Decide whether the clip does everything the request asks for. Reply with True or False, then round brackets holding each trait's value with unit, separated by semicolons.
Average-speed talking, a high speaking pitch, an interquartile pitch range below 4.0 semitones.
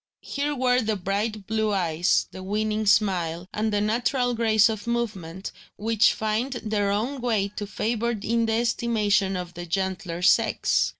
True (160 wpm; 215 Hz; 3.0 semitones)